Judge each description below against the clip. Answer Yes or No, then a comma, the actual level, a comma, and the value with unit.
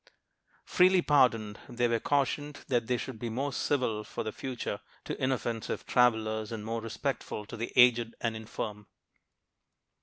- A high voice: No, low, 115 Hz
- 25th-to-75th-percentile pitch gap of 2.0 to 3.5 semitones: Yes, average, 2.8 semitones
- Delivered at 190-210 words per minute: No, average, 150 wpm